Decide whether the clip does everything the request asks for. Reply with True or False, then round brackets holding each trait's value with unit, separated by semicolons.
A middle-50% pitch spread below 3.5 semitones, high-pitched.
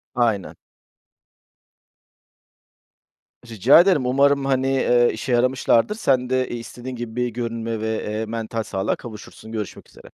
False (2.5 semitones; 120 Hz)